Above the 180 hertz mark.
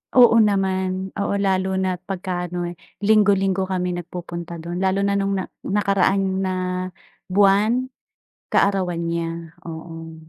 Yes: high, 190 Hz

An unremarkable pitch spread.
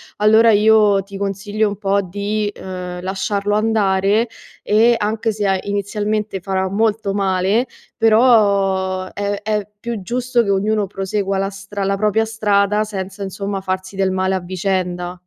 No: narrow, 1.9 semitones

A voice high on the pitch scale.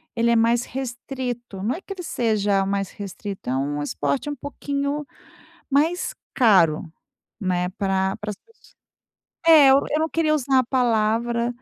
Yes: high, 235 Hz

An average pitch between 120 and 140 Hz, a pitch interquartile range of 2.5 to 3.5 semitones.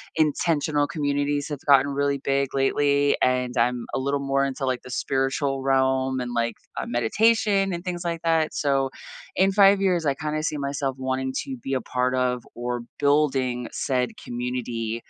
Yes: low, 135 Hz; average, 2.9 semitones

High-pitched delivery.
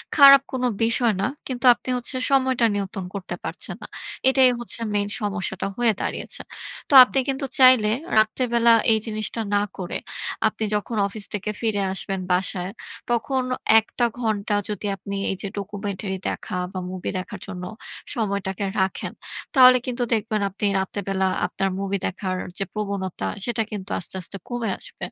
Yes: high, 210 Hz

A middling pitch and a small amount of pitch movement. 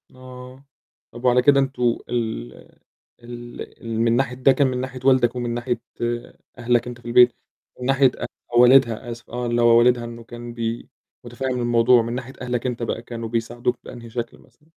No: low, 120 Hz; narrow, 1.2 semitones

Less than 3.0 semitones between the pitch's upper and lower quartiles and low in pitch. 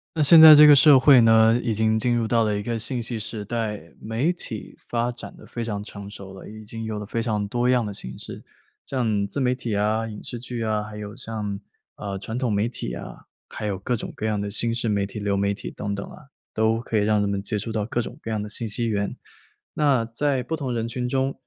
Yes: narrow, 2.6 semitones; low, 110 Hz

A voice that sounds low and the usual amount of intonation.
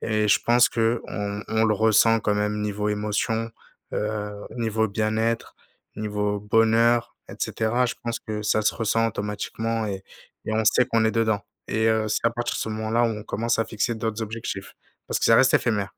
No: low, 110 Hz; narrow, 1.4 semitones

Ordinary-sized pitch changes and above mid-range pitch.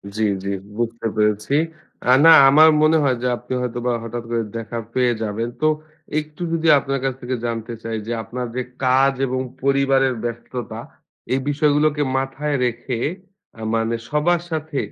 No: average, 3.6 semitones; low, 130 Hz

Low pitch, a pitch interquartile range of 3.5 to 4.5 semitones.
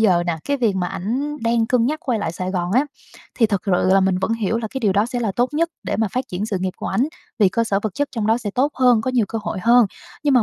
No: high, 225 Hz; average, 4.2 semitones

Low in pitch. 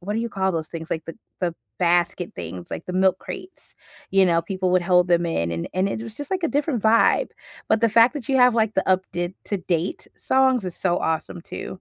No: medium, 185 Hz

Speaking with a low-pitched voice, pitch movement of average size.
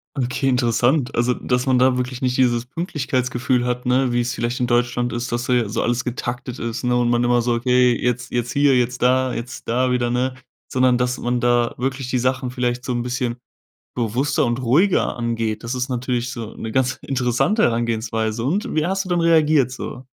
No: low, 125 Hz; narrow, 1.3 semitones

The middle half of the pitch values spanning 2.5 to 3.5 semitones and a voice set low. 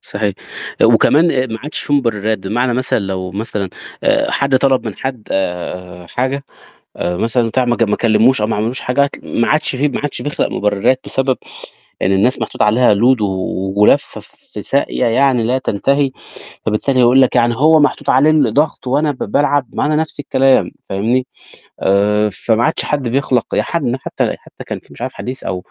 No: average, 4.5 semitones; low, 125 Hz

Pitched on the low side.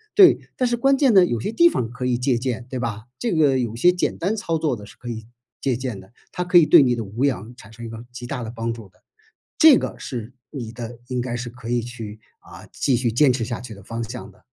Yes: low, 125 Hz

